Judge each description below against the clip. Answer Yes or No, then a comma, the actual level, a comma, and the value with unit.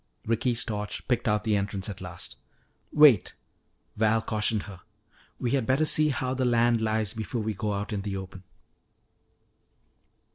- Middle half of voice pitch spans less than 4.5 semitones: Yes, average, 2.8 semitones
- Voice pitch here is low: Yes, low, 110 Hz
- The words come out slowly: No, average, 155 wpm